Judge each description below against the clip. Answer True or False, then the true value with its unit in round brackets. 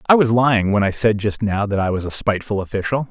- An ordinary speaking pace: False (270 wpm)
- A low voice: True (105 Hz)